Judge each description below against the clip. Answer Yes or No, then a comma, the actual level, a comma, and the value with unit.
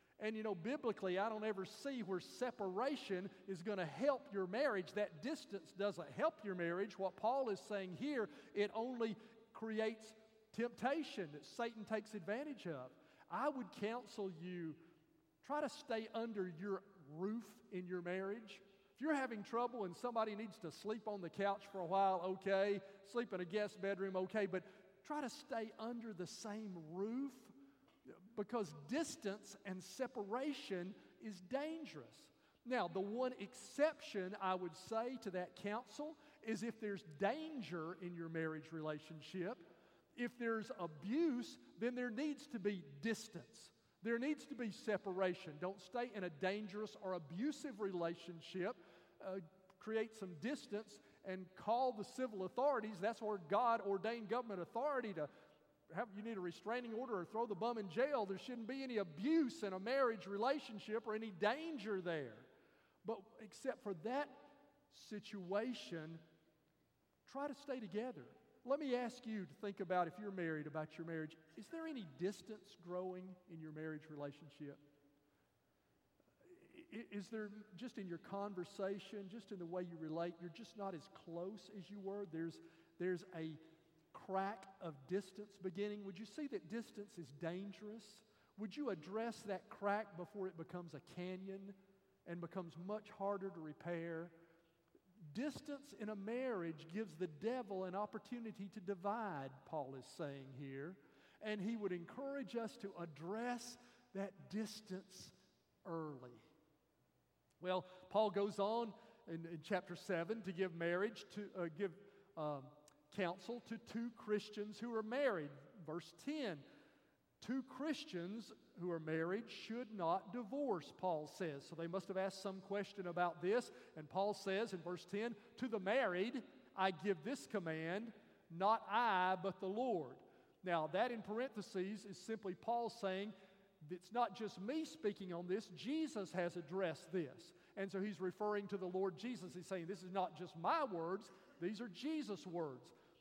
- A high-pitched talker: Yes, high, 200 Hz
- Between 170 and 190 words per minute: No, average, 155 wpm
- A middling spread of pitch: Yes, average, 4.0 semitones